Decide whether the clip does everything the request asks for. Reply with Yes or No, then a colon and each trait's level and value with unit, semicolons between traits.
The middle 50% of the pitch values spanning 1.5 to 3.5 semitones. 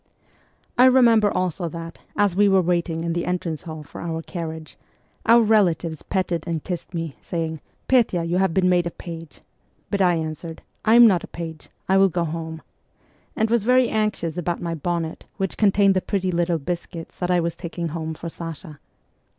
Yes: average, 2.8 semitones